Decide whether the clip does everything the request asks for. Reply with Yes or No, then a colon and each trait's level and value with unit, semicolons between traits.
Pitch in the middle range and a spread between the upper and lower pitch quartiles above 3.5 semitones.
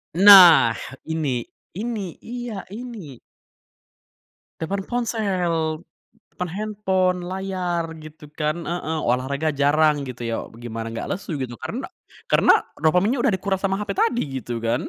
Yes: medium, 180 Hz; average, 4.5 semitones